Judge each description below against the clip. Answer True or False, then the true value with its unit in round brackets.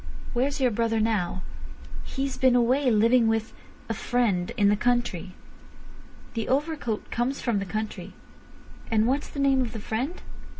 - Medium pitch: False (235 Hz)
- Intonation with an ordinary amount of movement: True (3.2 semitones)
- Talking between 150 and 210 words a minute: False (140 wpm)